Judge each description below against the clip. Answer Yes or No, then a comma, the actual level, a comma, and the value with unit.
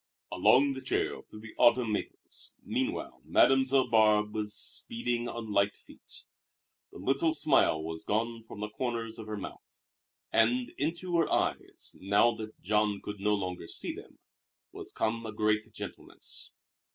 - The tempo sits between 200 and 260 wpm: No, average, 150 wpm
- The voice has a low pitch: Yes, low, 110 Hz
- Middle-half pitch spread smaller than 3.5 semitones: Yes, average, 3.0 semitones